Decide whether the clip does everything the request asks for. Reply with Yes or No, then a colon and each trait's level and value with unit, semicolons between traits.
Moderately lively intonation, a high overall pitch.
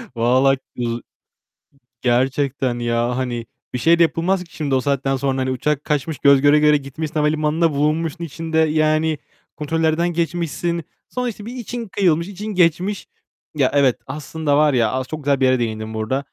No: average, 3.9 semitones; medium, 150 Hz